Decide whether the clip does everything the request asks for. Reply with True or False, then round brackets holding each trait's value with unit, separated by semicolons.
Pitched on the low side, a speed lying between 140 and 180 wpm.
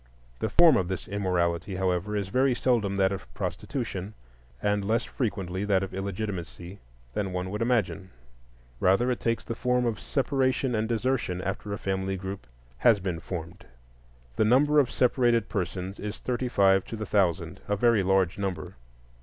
True (100 Hz; 160 wpm)